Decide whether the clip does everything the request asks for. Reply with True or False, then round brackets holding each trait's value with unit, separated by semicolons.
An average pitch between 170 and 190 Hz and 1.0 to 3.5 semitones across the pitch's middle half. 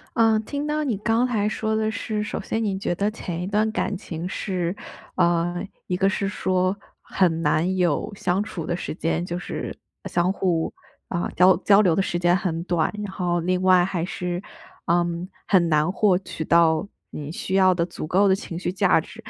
True (185 Hz; 2.6 semitones)